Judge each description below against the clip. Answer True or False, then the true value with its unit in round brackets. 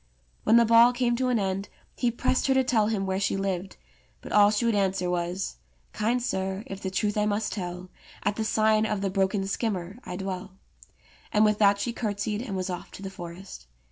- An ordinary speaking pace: False (215 wpm)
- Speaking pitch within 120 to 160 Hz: False (205 Hz)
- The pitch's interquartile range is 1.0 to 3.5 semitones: True (2.5 semitones)